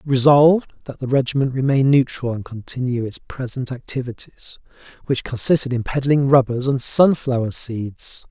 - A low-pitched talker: Yes, low, 130 Hz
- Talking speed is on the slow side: Yes, slow, 130 wpm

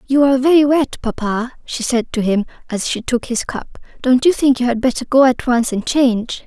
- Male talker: No, female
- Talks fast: Yes, fast, 230 wpm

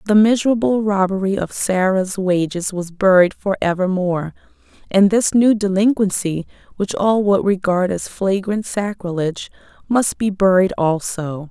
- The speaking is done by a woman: Yes, female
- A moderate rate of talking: No, slow, 130 wpm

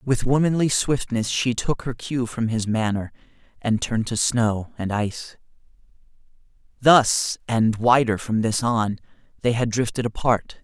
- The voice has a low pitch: Yes, low, 115 Hz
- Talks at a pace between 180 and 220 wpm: No, average, 145 wpm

